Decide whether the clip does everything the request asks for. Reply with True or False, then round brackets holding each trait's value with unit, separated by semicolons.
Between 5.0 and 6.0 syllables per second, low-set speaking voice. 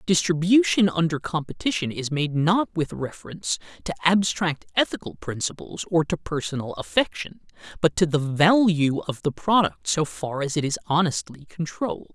False (5.1 syllables/s; 165 Hz)